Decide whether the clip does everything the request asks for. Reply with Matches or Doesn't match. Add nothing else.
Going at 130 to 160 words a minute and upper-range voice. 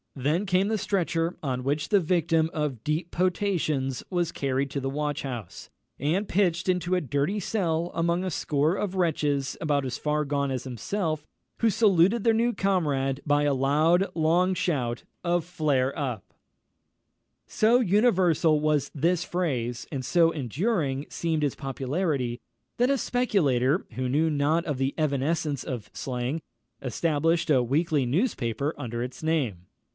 Doesn't match